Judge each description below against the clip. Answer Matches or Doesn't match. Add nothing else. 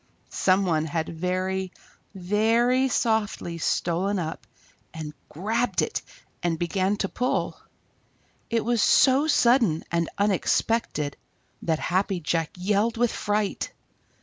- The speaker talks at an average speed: Doesn't match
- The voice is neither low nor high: Doesn't match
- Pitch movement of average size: Matches